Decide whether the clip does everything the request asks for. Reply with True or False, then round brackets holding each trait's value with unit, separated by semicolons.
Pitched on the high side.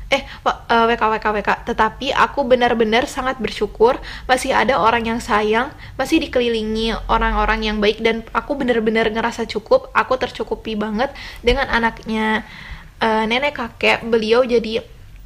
True (230 Hz)